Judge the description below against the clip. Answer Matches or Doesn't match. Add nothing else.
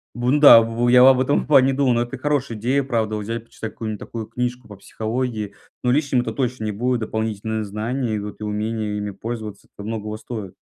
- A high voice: Doesn't match